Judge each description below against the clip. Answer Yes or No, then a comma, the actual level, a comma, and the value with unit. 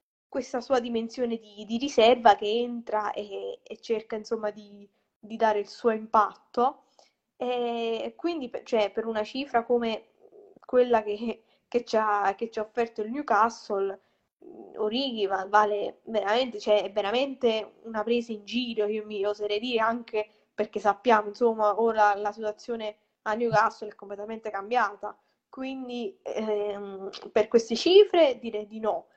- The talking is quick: No, average, 140 wpm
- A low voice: No, high, 225 Hz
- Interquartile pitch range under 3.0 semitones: Yes, narrow, 2.4 semitones